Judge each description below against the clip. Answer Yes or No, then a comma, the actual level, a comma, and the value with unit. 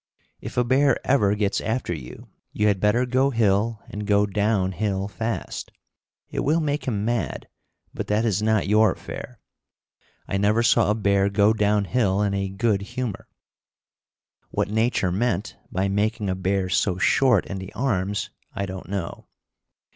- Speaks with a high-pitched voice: No, low, 105 Hz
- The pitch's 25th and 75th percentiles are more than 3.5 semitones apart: No, average, 2.8 semitones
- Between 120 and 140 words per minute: No, average, 165 wpm